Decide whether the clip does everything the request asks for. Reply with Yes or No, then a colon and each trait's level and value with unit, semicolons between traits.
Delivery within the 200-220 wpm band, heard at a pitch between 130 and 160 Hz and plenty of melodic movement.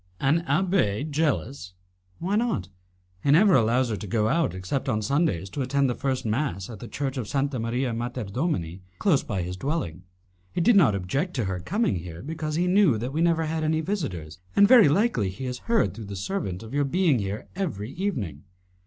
Yes: fast, 205 wpm; low, 135 Hz; wide, 8.1 semitones